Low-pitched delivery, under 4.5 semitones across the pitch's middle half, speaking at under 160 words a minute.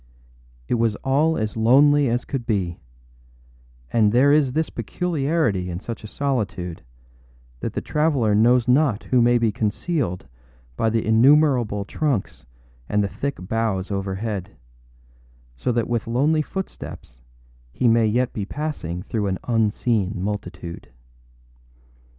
No: low, 115 Hz; average, 4.9 semitones; slow, 135 wpm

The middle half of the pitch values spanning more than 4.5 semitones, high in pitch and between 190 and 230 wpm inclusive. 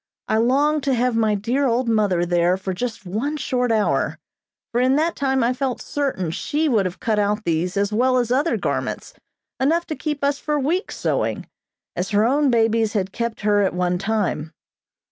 Yes: average, 5.0 semitones; high, 230 Hz; average, 195 wpm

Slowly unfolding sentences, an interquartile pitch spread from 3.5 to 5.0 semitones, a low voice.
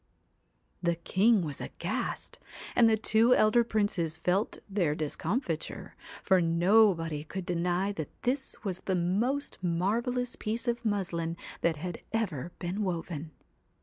No: slow, 130 wpm; average, 4.7 semitones; medium, 185 Hz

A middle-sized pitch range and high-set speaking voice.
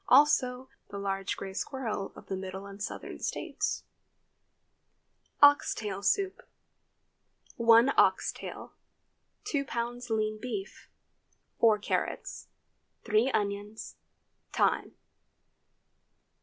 Yes: average, 3.9 semitones; high, 220 Hz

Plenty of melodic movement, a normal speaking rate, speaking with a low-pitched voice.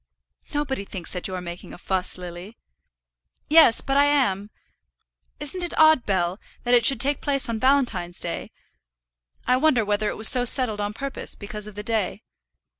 No: wide, 6.0 semitones; average, 180 wpm; high, 225 Hz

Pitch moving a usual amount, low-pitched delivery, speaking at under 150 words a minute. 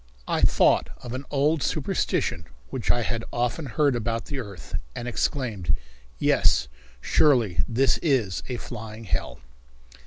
Yes: average, 3.9 semitones; low, 120 Hz; slow, 135 wpm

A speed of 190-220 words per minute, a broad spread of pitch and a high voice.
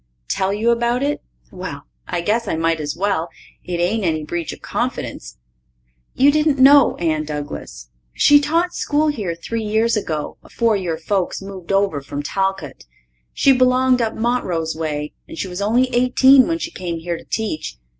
No: average, 175 wpm; wide, 7.2 semitones; high, 200 Hz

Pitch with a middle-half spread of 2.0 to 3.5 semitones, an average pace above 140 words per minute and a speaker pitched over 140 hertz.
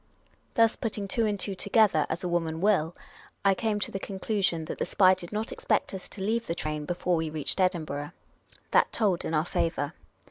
No: average, 4.3 semitones; fast, 205 wpm; medium, 185 Hz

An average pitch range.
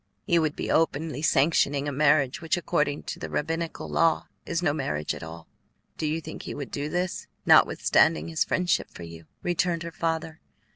Yes: average, 3.2 semitones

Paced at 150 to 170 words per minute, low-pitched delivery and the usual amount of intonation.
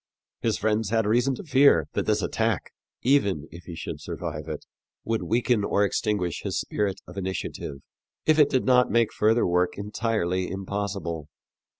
Yes: average, 165 wpm; low, 105 Hz; average, 4.6 semitones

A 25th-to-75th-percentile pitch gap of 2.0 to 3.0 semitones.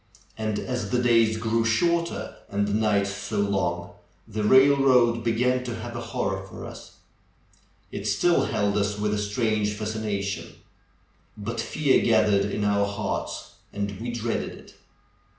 Yes: narrow, 2.6 semitones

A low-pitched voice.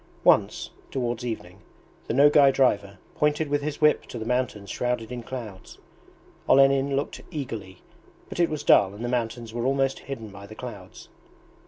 Yes: low, 125 Hz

